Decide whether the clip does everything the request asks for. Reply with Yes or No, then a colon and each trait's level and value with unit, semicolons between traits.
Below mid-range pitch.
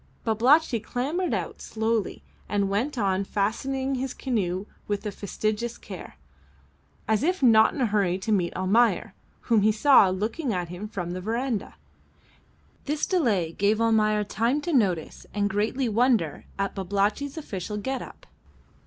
No: high, 215 Hz